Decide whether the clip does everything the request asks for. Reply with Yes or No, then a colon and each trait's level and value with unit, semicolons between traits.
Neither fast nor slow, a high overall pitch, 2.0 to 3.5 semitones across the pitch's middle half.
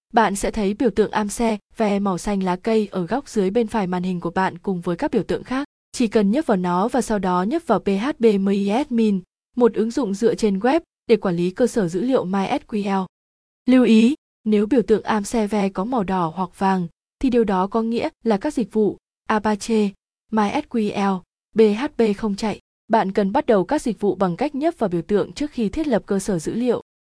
Yes: average, 220 wpm; high, 215 Hz; average, 3.2 semitones